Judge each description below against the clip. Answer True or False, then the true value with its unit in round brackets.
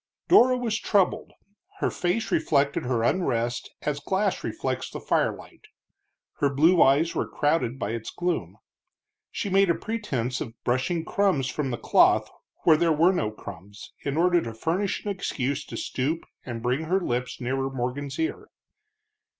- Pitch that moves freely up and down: True (6.2 semitones)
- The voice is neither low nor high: True (145 Hz)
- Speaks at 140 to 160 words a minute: True (155 wpm)